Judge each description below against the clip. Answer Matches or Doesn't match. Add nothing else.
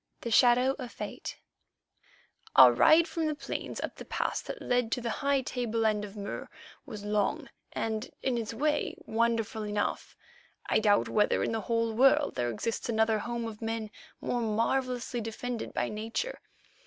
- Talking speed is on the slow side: Doesn't match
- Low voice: Doesn't match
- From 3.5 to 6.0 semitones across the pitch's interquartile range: Doesn't match